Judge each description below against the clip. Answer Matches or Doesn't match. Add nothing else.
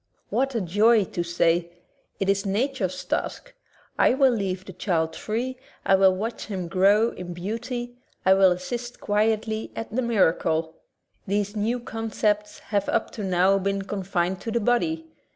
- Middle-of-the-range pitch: Doesn't match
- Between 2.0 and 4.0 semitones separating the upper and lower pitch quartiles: Matches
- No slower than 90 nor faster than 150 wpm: Doesn't match